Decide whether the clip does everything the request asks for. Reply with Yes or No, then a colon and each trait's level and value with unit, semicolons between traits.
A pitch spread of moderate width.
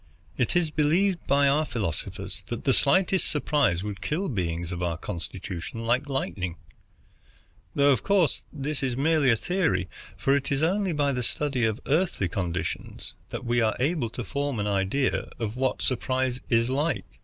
No: wide, 6.2 semitones